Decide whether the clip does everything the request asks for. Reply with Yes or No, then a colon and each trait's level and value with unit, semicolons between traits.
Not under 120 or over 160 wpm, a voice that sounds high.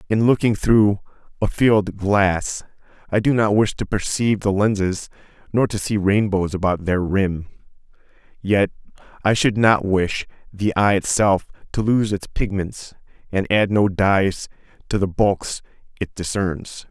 No: average, 150 wpm; low, 100 Hz